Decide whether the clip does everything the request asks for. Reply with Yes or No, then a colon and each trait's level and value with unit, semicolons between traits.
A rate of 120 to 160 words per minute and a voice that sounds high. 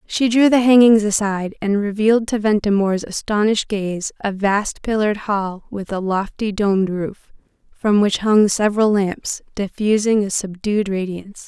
Yes: average, 150 wpm; high, 205 Hz